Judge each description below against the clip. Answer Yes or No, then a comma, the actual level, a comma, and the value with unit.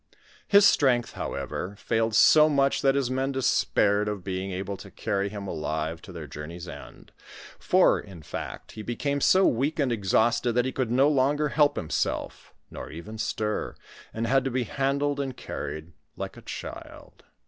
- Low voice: Yes, low, 115 Hz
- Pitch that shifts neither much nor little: No, wide, 5.9 semitones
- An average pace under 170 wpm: No, average, 175 wpm